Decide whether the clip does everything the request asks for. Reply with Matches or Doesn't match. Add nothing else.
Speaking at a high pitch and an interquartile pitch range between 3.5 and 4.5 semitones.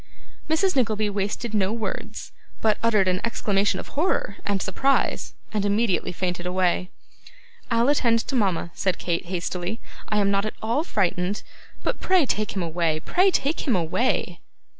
Matches